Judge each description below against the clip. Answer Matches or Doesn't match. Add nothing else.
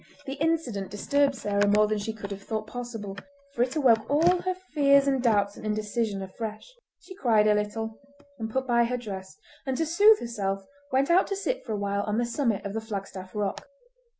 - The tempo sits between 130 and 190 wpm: Doesn't match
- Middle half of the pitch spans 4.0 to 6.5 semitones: Matches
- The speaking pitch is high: Matches